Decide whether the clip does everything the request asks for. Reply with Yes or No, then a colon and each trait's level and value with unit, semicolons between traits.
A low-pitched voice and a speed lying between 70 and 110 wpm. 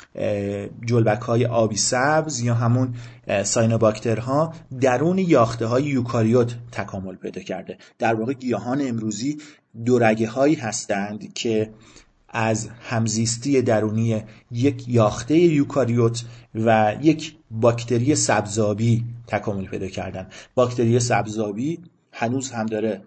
Yes: low, 115 Hz; slow, 105 wpm